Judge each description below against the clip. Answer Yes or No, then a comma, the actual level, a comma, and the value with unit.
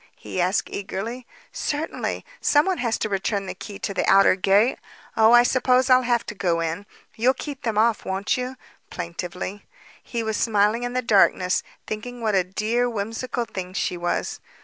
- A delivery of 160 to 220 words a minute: Yes, average, 175 wpm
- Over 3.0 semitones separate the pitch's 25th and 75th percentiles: Yes, average, 4.1 semitones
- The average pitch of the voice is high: Yes, high, 215 Hz